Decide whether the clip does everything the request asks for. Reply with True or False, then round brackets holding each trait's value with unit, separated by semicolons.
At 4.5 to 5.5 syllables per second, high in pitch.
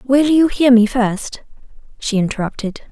True (4.6 syllables/s; 240 Hz)